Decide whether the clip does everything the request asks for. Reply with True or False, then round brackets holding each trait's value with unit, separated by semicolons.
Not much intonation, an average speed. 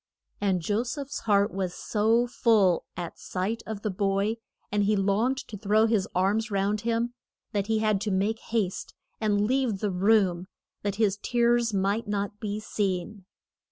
True (2.3 semitones; 170 wpm)